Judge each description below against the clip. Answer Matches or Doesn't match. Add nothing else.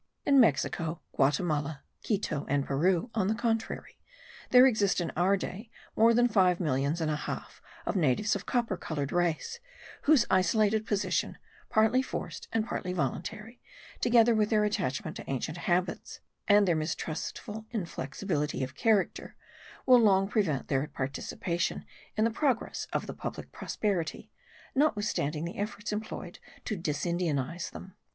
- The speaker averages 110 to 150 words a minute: Matches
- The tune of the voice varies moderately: Doesn't match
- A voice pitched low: Doesn't match